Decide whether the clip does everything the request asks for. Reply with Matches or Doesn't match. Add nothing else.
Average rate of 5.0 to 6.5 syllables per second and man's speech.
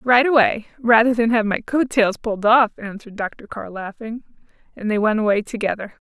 Doesn't match